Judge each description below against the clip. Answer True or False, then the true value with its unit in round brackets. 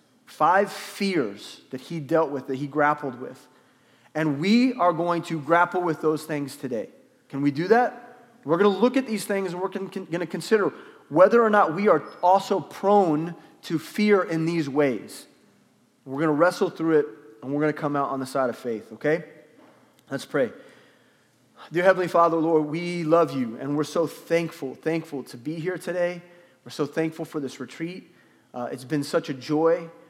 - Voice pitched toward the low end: False (165 Hz)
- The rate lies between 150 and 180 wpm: False (190 wpm)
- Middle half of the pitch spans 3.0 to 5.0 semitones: True (3.5 semitones)